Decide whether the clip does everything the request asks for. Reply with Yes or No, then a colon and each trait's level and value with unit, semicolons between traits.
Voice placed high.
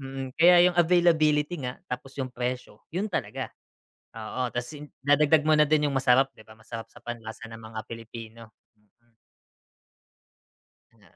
No: low, 130 Hz